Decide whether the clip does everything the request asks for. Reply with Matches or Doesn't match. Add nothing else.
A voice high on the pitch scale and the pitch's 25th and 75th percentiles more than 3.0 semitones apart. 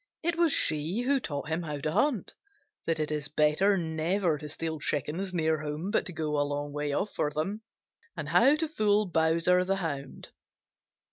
Doesn't match